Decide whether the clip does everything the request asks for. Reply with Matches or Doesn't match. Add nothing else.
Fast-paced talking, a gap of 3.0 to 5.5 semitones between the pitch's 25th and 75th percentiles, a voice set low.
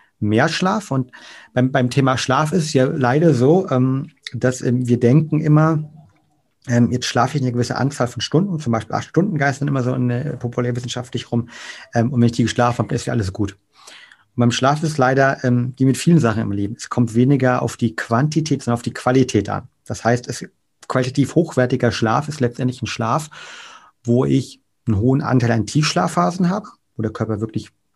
Matches